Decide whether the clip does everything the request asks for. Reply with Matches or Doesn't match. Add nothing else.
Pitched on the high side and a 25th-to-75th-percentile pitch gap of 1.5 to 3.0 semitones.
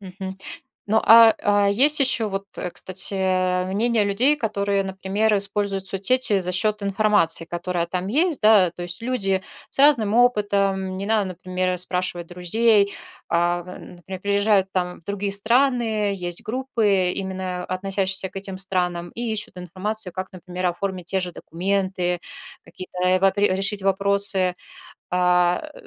Matches